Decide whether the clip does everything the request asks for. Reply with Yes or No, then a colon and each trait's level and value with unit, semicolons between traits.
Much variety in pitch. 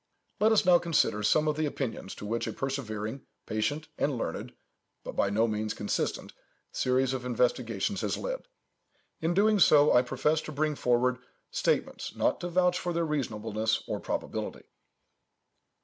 Yes: wide, 6.0 semitones